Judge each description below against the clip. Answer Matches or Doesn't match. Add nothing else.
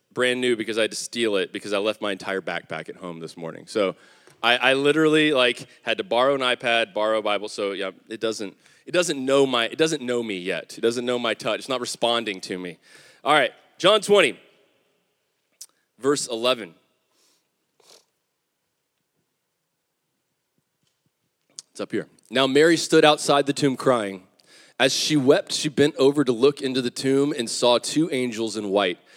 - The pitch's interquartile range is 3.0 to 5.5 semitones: Matches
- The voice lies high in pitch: Doesn't match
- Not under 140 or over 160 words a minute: Doesn't match